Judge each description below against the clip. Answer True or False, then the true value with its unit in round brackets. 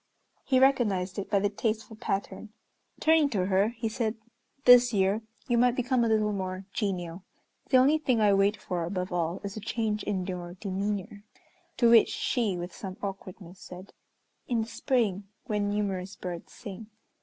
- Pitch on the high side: True (205 Hz)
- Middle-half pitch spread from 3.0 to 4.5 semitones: True (3.6 semitones)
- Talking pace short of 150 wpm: False (170 wpm)